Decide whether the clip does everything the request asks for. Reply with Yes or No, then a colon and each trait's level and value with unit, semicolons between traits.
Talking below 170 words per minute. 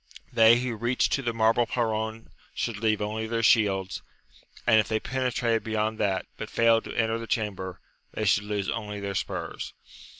No: average, 175 wpm